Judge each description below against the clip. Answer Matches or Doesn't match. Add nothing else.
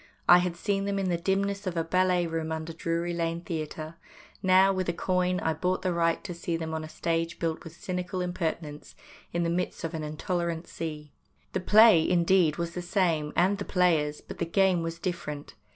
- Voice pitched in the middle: Matches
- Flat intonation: Matches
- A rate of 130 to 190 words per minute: Doesn't match